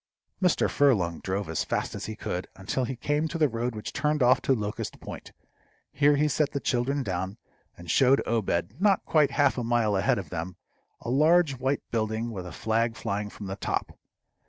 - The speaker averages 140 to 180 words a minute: No, average, 200 wpm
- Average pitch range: No, wide, 5.7 semitones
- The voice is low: Yes, low, 120 Hz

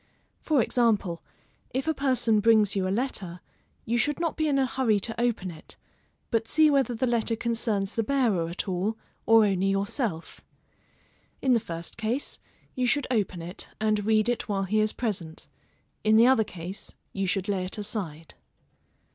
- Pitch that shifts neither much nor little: Yes, average, 3.9 semitones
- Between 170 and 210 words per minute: Yes, average, 175 wpm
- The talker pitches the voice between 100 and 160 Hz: No, high, 220 Hz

